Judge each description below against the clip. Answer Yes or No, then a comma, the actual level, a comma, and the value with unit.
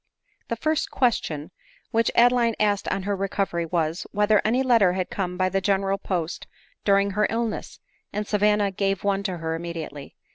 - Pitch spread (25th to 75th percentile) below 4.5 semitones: Yes, average, 2.7 semitones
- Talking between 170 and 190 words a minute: Yes, average, 175 wpm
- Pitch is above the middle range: Yes, high, 195 Hz